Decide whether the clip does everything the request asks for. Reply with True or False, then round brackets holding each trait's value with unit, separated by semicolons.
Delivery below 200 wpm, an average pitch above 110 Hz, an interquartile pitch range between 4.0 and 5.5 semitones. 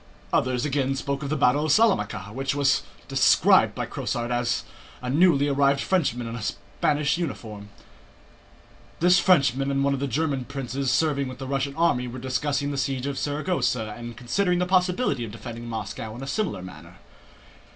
False (170 wpm; 135 Hz; 3.4 semitones)